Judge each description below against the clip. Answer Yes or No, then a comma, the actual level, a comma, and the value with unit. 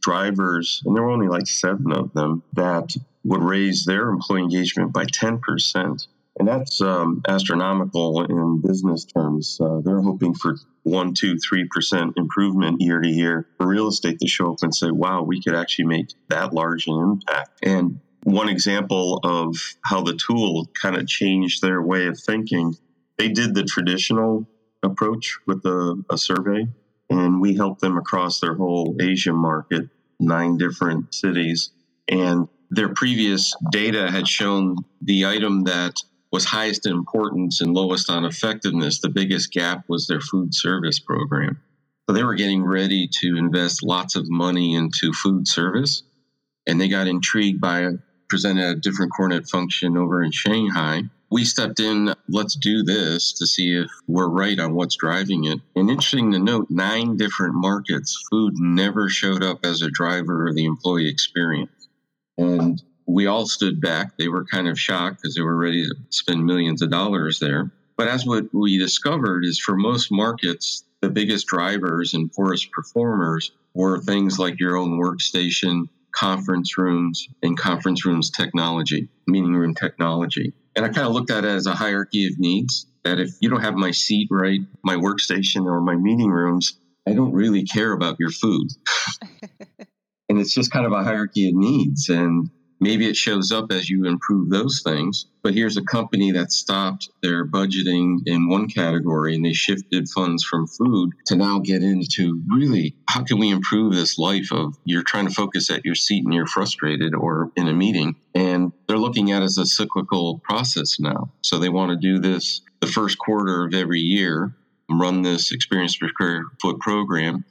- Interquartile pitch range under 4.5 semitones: Yes, narrow, 2.5 semitones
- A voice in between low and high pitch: No, very low, 90 Hz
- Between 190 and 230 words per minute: No, average, 175 wpm